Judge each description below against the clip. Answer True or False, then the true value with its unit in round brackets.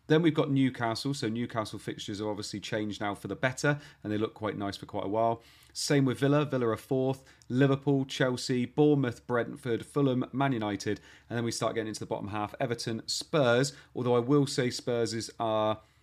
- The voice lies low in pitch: True (120 Hz)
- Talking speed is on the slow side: False (200 wpm)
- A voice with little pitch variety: False (3.8 semitones)